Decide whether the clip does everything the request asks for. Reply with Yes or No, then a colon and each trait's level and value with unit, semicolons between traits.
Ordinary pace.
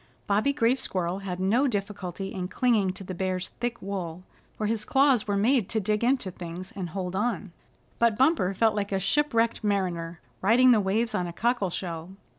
Yes: average, 190 wpm